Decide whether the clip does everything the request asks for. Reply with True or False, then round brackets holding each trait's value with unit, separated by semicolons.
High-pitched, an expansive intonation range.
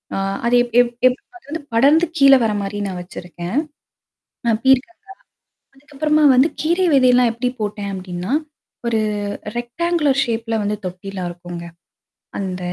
True (240 Hz; 5.9 semitones)